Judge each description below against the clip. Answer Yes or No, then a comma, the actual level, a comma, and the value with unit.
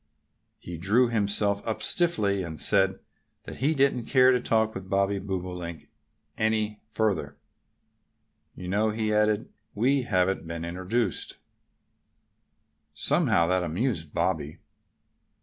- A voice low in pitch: Yes, low, 100 Hz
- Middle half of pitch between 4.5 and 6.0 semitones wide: No, average, 3.4 semitones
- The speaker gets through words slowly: Yes, slow, 115 wpm